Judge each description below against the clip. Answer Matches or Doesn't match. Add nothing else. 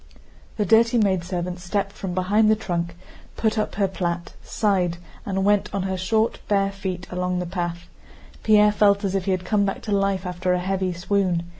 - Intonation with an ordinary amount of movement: Doesn't match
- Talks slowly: Doesn't match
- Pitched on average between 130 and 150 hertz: Doesn't match